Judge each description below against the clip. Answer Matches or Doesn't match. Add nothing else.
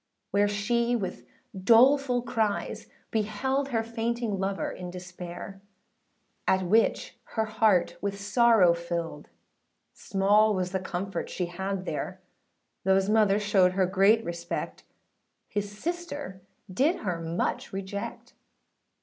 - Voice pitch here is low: Doesn't match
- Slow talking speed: Matches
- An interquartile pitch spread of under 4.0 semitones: Matches